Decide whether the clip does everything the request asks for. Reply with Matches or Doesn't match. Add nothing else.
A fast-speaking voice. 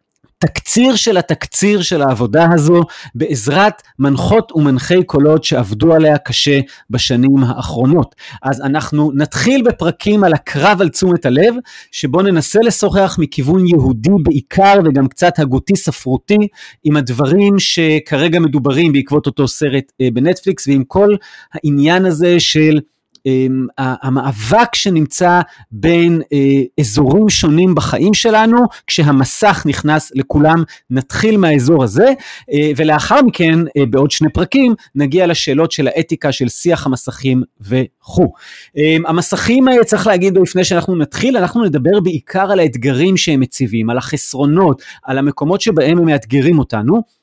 Doesn't match